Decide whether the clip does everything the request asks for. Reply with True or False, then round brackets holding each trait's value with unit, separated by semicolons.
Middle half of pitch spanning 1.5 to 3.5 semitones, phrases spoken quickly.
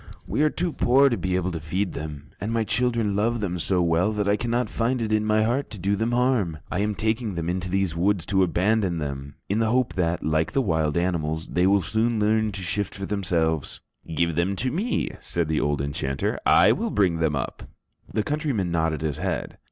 False (5.0 semitones; 220 wpm)